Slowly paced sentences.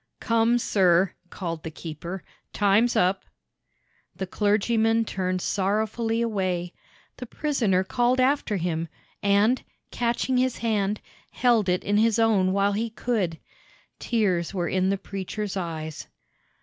Yes: slow, 125 wpm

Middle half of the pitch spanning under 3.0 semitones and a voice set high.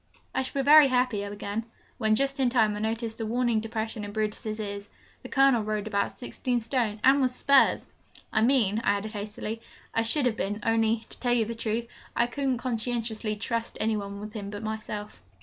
Yes: narrow, 2.6 semitones; high, 225 Hz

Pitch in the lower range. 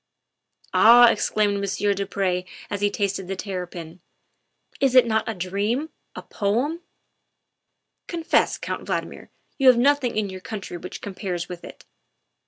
No: high, 205 Hz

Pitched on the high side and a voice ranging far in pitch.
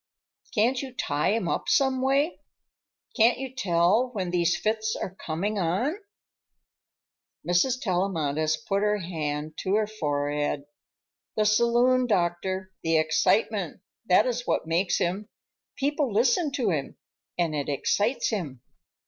Yes: high, 195 Hz; wide, 6.2 semitones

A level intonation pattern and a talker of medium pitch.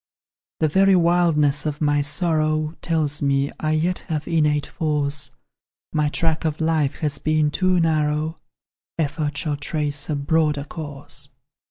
Yes: narrow, 1.7 semitones; medium, 155 Hz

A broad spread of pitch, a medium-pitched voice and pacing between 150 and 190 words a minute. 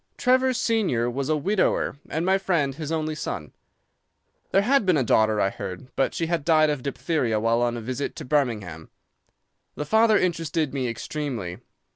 Yes: wide, 6.3 semitones; medium, 150 Hz; average, 175 wpm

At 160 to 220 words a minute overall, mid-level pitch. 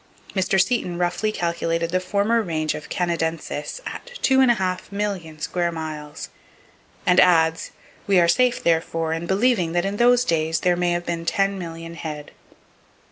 Yes: average, 175 wpm; medium, 175 Hz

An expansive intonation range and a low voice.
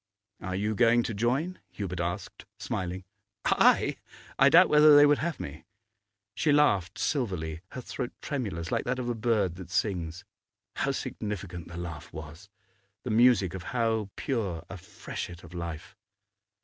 Yes: wide, 6.0 semitones; low, 100 Hz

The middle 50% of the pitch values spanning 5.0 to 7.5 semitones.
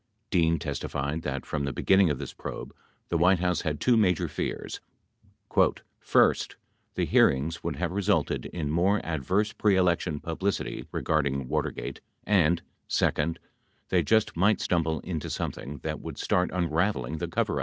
No: average, 3.6 semitones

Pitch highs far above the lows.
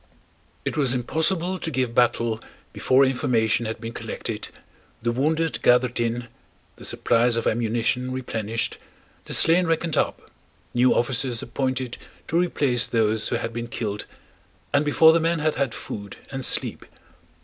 No: average, 3.7 semitones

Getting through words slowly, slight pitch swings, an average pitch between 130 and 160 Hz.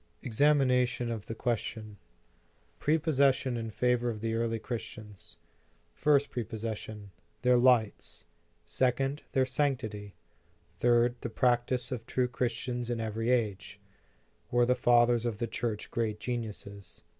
No: slow, 120 wpm; narrow, 2.2 semitones; low, 120 Hz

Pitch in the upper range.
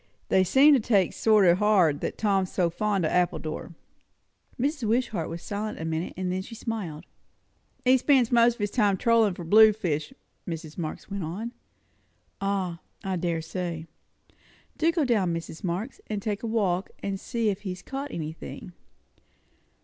Yes: high, 195 Hz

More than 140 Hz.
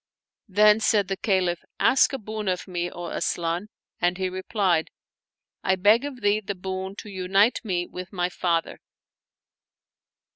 Yes: high, 190 Hz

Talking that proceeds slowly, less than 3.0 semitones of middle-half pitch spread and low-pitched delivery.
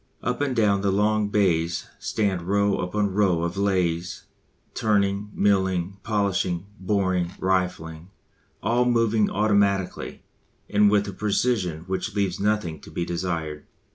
Yes: slow, 130 wpm; narrow, 2.5 semitones; low, 100 Hz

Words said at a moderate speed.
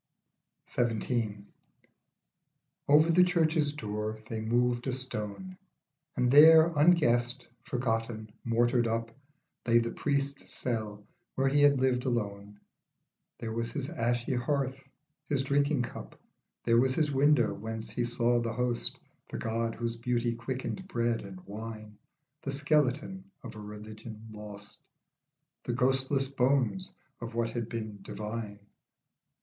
No: slow, 130 wpm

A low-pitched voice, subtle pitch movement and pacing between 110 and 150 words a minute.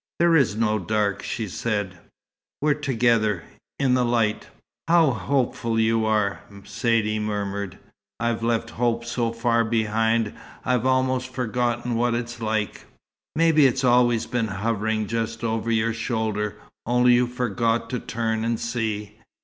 Yes: low, 115 Hz; narrow, 2.1 semitones; average, 140 wpm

